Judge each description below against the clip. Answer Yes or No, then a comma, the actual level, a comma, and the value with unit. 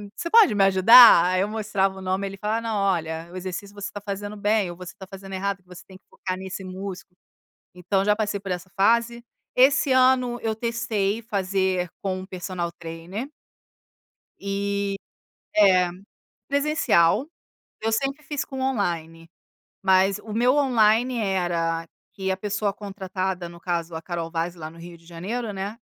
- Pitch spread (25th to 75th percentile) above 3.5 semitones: No, average, 3.2 semitones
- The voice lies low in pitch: No, high, 195 Hz